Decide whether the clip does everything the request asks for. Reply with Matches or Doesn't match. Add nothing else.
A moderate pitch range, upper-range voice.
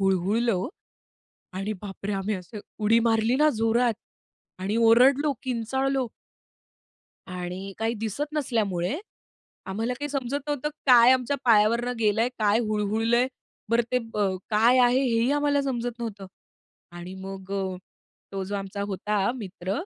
Matches